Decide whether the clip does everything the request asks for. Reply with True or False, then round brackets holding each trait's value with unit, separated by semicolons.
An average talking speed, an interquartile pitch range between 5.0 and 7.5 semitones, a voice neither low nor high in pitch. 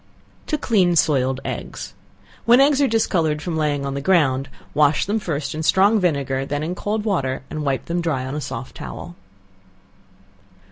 True (180 wpm; 5.6 semitones; 155 Hz)